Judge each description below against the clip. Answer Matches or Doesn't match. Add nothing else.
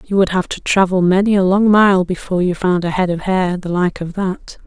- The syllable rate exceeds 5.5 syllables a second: Doesn't match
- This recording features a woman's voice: Matches